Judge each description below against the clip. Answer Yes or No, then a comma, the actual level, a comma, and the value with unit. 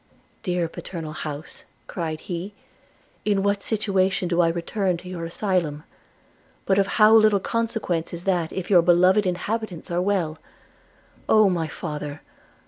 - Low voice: No, medium, 180 Hz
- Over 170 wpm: No, average, 150 wpm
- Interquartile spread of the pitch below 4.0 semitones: Yes, average, 3.2 semitones